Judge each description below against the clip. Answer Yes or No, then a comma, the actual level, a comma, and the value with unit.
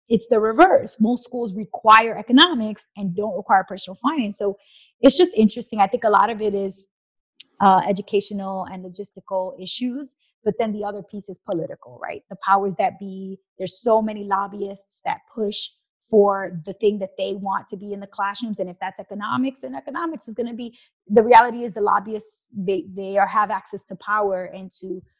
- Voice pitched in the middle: No, high, 205 Hz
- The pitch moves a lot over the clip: No, average, 2.7 semitones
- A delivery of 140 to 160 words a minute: No, average, 195 wpm